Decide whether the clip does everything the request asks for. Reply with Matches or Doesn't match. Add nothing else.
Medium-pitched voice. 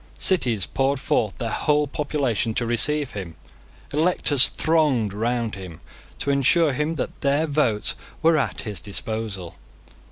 Doesn't match